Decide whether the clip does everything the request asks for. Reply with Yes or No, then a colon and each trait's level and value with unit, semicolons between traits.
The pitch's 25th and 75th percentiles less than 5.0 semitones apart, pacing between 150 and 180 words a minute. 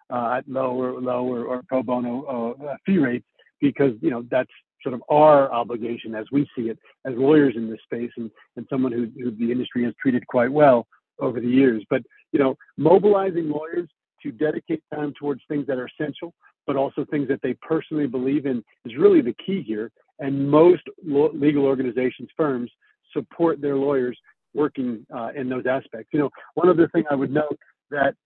No: average, 3.3 semitones; average, 195 wpm